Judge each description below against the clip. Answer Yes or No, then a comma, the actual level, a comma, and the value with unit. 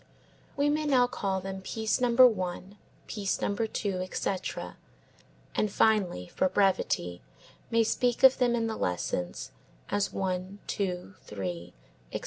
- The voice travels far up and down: No, average, 4.0 semitones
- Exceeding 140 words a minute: No, slow, 135 wpm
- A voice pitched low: No, high, 200 Hz